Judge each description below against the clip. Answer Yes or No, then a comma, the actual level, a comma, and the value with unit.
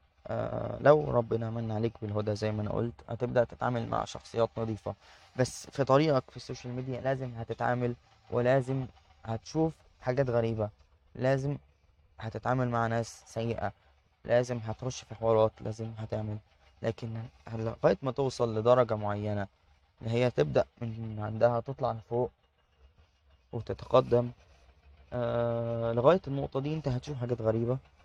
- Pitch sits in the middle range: No, low, 115 Hz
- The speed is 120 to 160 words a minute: Yes, average, 125 wpm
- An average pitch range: Yes, average, 3.1 semitones